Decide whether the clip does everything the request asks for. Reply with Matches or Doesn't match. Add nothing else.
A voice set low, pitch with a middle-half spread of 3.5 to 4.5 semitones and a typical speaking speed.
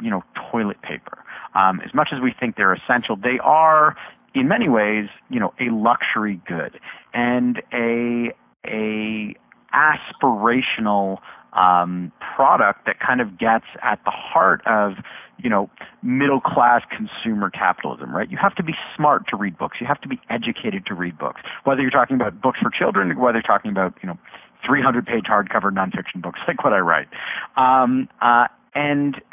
Matches